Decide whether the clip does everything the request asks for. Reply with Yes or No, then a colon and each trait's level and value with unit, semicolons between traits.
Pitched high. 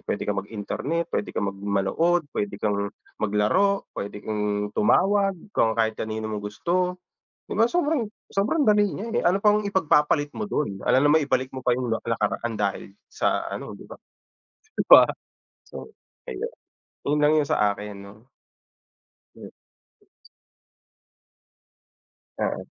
No: low, 130 Hz